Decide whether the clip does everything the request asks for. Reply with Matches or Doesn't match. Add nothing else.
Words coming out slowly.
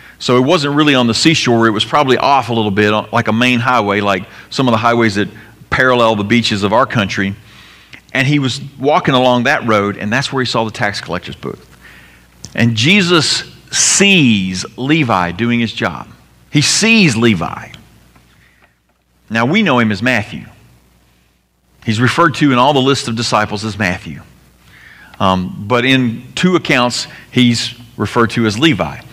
Doesn't match